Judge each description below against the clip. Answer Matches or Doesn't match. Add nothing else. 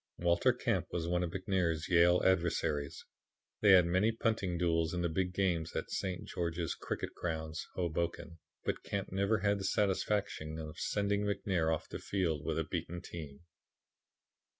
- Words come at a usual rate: Matches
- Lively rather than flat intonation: Doesn't match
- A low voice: Matches